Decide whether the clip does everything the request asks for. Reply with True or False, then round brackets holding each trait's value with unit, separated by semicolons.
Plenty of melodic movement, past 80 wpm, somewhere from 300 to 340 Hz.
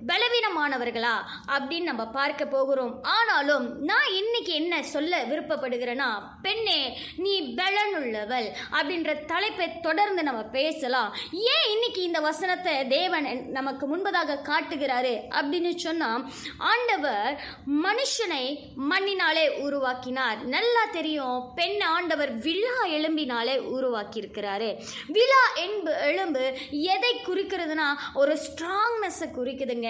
True (5.7 semitones; 100 wpm; 310 Hz)